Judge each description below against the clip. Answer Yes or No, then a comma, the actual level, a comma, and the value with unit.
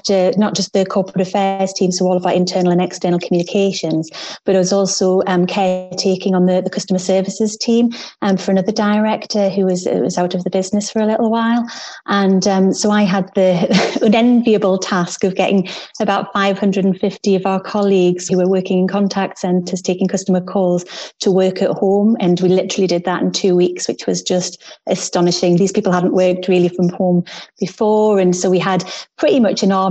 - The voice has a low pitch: No, high, 190 Hz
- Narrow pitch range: Yes, narrow, 1.5 semitones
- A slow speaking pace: No, average, 200 wpm